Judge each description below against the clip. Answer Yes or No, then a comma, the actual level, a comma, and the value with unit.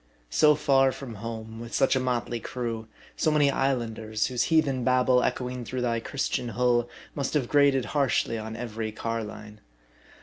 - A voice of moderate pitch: No, low, 125 Hz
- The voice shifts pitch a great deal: No, average, 2.8 semitones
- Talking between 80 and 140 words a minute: No, average, 160 wpm